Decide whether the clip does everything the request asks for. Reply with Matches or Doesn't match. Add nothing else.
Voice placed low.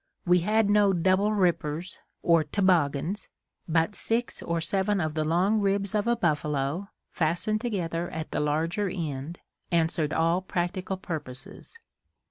Doesn't match